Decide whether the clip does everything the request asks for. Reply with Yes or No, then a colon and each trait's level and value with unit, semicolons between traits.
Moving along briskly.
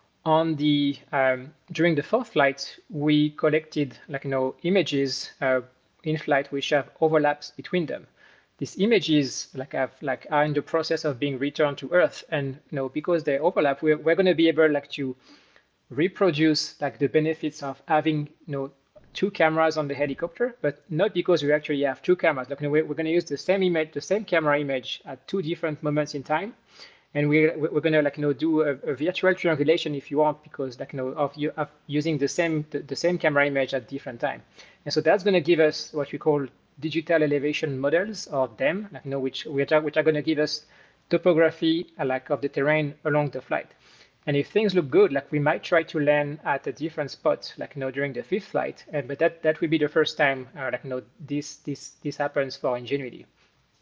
Yes: fast, 220 wpm